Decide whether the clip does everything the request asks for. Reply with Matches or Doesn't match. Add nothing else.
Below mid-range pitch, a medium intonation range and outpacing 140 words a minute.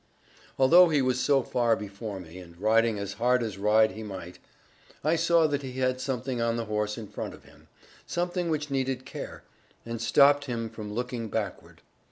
Matches